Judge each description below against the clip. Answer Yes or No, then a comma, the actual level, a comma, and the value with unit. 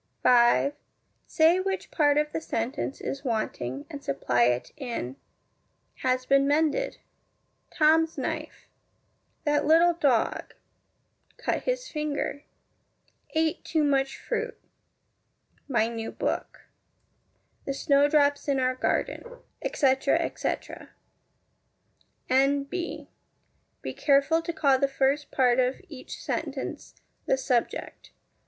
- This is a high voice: Yes, very high, 280 Hz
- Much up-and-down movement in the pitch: No, average, 3.4 semitones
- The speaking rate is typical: No, slow, 105 wpm